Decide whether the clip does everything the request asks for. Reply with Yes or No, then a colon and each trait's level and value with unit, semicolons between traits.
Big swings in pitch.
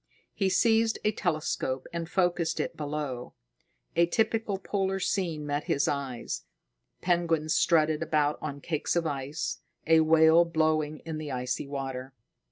No: average, 3.1 semitones